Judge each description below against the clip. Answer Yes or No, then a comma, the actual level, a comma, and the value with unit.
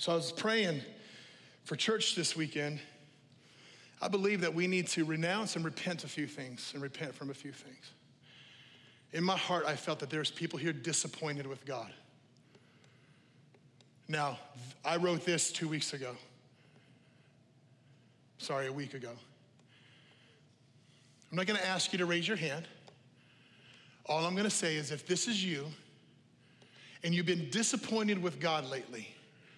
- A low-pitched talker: No, medium, 150 Hz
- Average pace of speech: Yes, average, 150 wpm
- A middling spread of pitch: Yes, average, 4.2 semitones